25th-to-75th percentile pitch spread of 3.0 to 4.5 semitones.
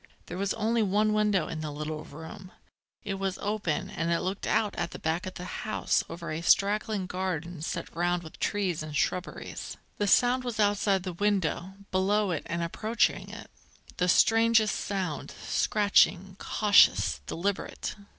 Yes: average, 3.5 semitones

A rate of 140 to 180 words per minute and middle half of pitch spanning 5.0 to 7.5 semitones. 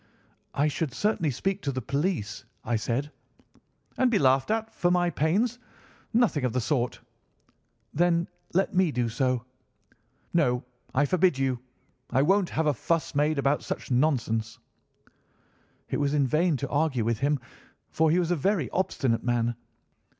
Yes: average, 155 wpm; wide, 5.5 semitones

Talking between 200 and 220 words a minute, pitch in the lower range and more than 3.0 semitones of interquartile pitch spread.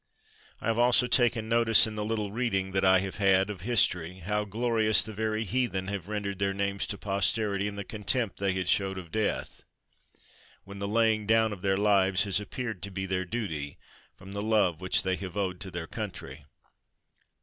No: fast, 205 wpm; low, 100 Hz; narrow, 2.5 semitones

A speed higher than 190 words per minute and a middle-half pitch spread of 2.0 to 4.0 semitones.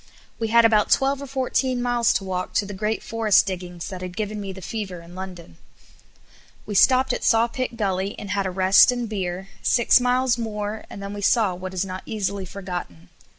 Yes: average, 200 wpm; average, 3.7 semitones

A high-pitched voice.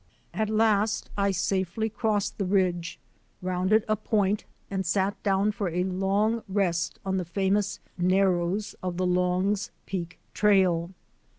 Yes: high, 195 Hz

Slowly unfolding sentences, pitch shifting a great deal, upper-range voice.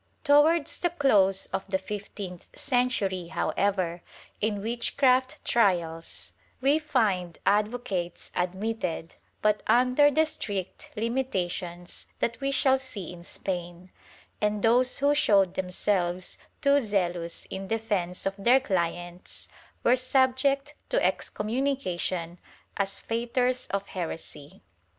Yes: slow, 115 wpm; wide, 5.9 semitones; high, 205 Hz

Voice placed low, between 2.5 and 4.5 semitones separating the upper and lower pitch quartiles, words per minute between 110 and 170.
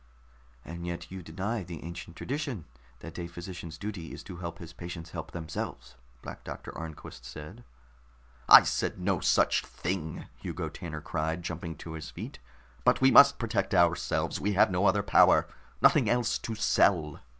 Yes: very low, 85 Hz; average, 3.3 semitones; average, 165 wpm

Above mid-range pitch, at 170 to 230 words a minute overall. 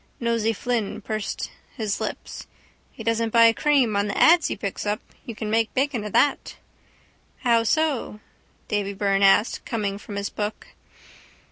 No: high, 220 Hz; average, 155 wpm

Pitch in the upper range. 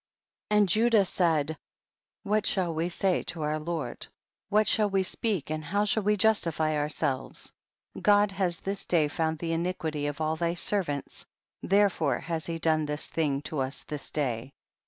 No: medium, 165 Hz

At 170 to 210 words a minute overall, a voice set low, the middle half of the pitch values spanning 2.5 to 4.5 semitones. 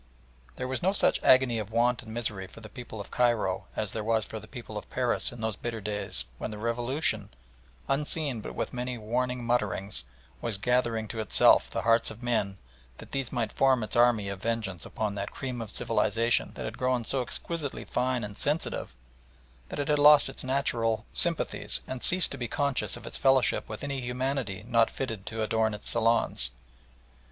Yes: average, 195 wpm; low, 115 Hz; average, 2.9 semitones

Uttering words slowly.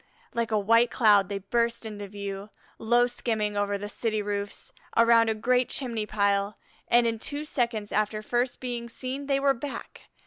No: average, 175 wpm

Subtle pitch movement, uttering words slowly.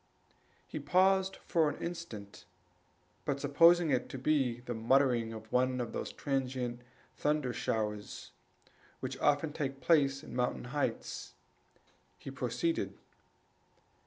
No: average, 4.0 semitones; slow, 120 wpm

